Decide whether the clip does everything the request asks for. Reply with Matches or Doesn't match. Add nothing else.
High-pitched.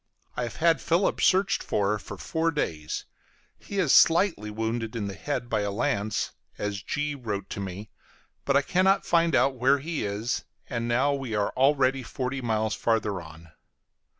Doesn't match